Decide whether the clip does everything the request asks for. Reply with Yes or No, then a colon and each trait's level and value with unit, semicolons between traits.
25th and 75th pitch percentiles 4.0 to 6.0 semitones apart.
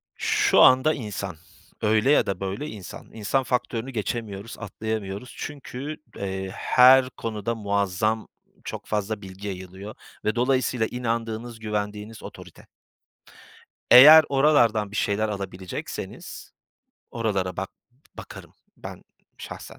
No: average, 3.6 semitones